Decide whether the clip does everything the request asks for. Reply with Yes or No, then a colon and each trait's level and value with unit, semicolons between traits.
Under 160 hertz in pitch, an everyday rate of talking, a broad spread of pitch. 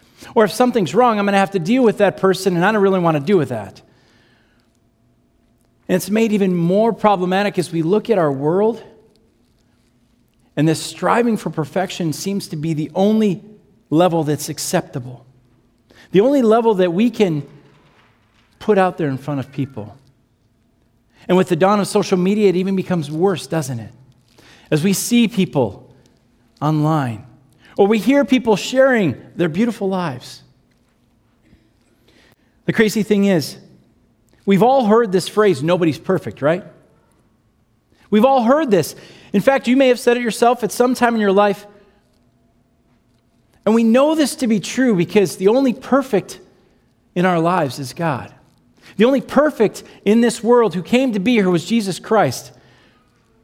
No: medium, 180 Hz; average, 165 wpm; wide, 8.7 semitones